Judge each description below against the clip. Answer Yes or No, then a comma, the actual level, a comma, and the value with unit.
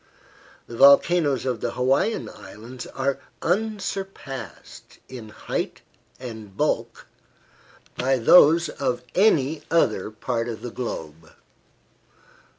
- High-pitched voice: No, low, 130 Hz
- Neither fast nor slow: No, slow, 100 wpm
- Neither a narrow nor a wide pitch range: No, wide, 5.7 semitones